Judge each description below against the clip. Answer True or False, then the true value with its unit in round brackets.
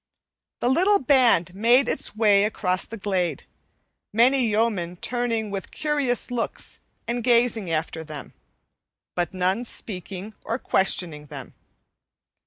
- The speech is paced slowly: True (120 wpm)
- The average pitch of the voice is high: True (215 Hz)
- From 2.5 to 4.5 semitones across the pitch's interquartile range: False (5.0 semitones)